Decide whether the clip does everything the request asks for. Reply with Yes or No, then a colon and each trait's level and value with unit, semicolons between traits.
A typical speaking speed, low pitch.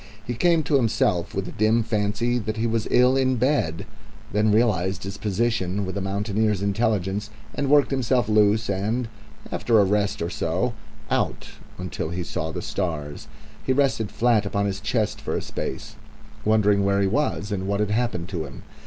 Yes: average, 180 wpm; low, 105 Hz